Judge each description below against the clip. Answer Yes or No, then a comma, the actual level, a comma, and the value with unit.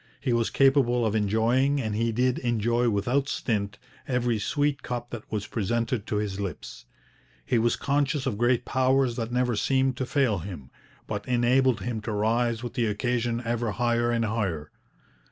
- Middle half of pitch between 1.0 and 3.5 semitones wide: Yes, average, 2.7 semitones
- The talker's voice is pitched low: Yes, low, 120 Hz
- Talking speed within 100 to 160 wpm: No, average, 170 wpm